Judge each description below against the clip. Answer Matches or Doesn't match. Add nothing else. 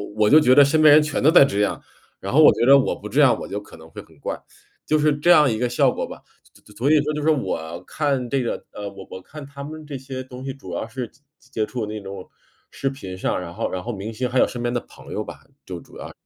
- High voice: Doesn't match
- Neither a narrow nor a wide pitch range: Doesn't match